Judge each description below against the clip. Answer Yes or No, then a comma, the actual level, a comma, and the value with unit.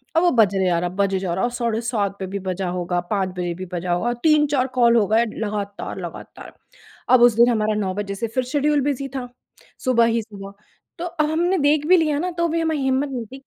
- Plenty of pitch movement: Yes, wide, 6.6 semitones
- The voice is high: Yes, high, 235 Hz